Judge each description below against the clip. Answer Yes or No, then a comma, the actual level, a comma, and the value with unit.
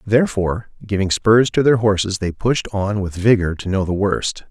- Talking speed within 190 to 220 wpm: Yes, average, 200 wpm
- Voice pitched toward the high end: No, low, 100 Hz